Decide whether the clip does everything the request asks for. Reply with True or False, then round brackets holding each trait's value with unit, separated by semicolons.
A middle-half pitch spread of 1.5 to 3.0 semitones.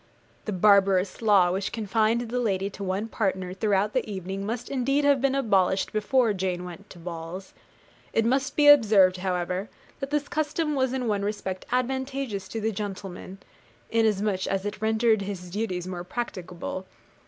False (4.0 semitones)